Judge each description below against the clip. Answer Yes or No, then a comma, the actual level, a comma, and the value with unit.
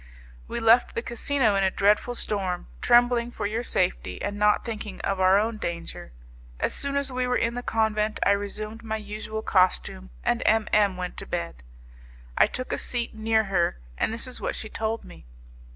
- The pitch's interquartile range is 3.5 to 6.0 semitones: No, average, 2.8 semitones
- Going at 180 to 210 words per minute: Yes, average, 195 wpm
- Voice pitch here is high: Yes, high, 215 Hz